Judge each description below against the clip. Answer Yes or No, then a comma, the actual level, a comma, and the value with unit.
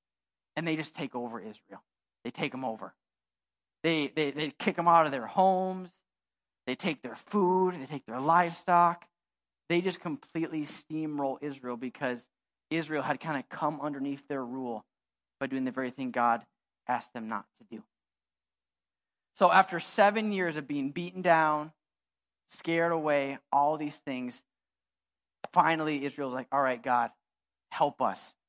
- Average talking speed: Yes, average, 155 wpm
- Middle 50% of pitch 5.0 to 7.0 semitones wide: Yes, average, 5.3 semitones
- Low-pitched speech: No, medium, 145 Hz